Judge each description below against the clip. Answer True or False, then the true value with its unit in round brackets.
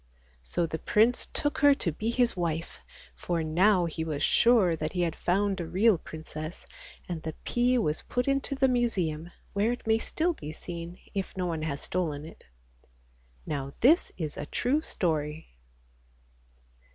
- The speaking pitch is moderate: True (175 Hz)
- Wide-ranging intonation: True (6.6 semitones)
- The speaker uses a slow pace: False (165 wpm)